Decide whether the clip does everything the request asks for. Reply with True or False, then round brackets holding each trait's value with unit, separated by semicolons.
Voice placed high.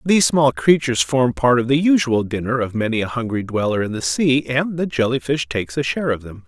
False (125 Hz)